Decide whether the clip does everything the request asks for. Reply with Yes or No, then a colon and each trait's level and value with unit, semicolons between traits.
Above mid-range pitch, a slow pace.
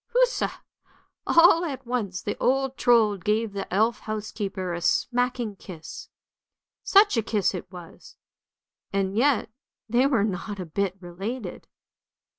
Yes: high, 215 Hz; slow, 130 wpm